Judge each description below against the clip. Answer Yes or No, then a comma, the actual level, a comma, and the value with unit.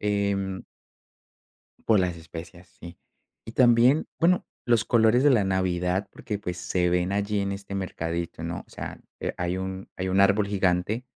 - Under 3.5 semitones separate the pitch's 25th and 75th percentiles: Yes, average, 2.8 semitones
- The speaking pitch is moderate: No, very low, 95 Hz